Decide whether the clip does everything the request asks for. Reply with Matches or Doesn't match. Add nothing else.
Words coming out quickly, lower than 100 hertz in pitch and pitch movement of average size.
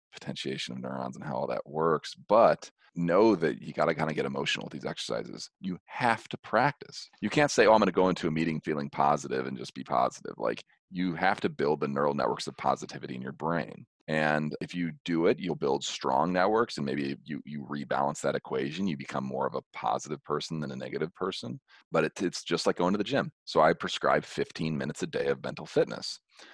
Matches